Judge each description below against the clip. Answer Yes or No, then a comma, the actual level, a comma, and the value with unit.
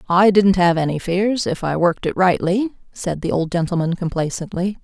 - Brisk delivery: No, average, 185 wpm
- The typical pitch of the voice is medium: Yes, medium, 180 Hz